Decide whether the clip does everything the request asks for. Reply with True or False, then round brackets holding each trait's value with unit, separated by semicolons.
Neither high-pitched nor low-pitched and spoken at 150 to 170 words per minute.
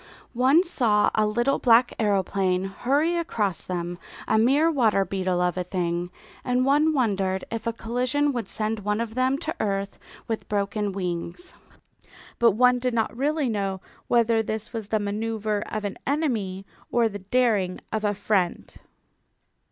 False (220 Hz; 160 wpm)